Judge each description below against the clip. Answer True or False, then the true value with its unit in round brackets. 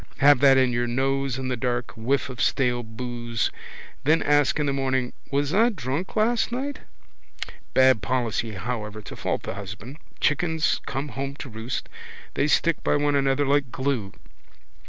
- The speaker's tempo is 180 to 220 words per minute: False (165 wpm)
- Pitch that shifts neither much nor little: True (3.1 semitones)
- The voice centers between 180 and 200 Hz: False (130 Hz)